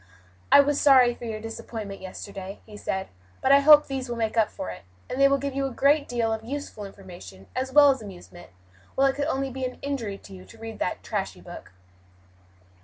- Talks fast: Yes, fast, 220 wpm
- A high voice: Yes, high, 240 Hz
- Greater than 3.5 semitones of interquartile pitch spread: Yes, average, 5.2 semitones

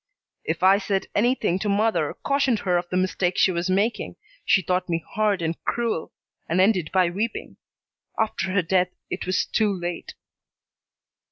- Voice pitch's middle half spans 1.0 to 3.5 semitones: Yes, average, 3.1 semitones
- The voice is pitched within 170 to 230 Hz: Yes, high, 190 Hz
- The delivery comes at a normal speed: Yes, average, 165 wpm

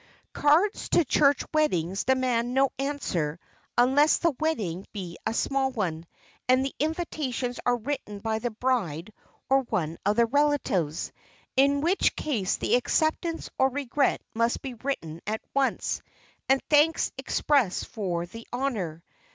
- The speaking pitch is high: Yes, very high, 250 Hz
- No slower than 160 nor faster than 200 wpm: No, average, 140 wpm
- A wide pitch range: Yes, wide, 5.8 semitones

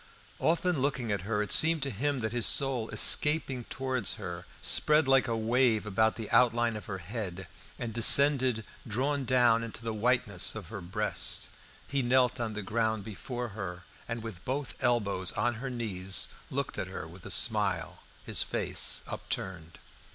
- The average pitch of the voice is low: Yes, low, 115 Hz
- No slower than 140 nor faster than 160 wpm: No, average, 170 wpm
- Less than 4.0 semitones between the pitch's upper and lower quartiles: Yes, average, 3.6 semitones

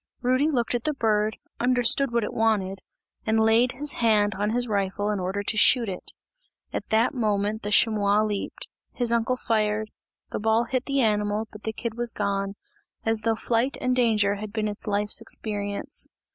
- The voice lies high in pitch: Yes, high, 220 Hz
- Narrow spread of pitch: Yes, narrow, 2.3 semitones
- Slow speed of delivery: No, average, 185 wpm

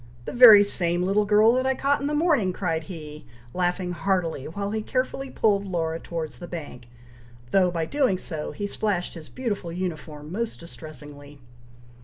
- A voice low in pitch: No, medium, 180 Hz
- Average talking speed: Yes, average, 170 wpm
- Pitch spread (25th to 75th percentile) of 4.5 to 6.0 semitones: Yes, average, 4.9 semitones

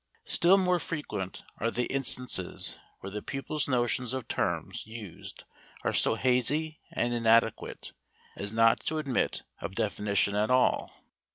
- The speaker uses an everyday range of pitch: Yes, average, 4.5 semitones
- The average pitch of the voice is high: No, low, 120 Hz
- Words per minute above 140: No, slow, 135 wpm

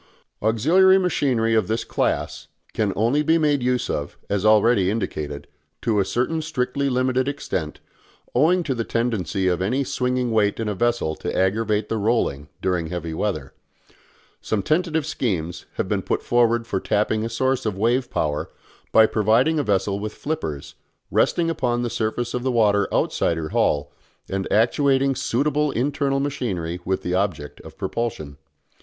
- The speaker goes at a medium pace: Yes, average, 160 wpm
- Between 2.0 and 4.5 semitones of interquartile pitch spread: No, average, 5.2 semitones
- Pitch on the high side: No, low, 115 Hz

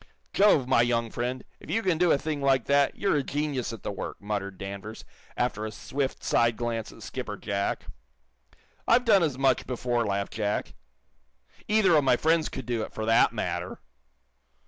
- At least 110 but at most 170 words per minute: No, average, 185 wpm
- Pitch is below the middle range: Yes, low, 125 Hz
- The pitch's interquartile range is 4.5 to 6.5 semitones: Yes, average, 5.0 semitones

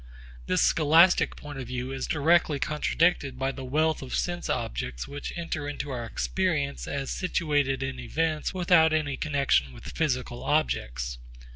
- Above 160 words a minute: No, average, 150 wpm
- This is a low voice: No, medium, 145 Hz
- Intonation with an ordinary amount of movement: Yes, average, 3.5 semitones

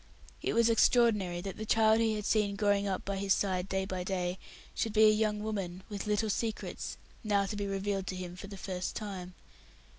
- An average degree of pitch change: No, narrow, 2.1 semitones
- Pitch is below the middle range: No, high, 200 Hz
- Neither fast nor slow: No, fast, 210 wpm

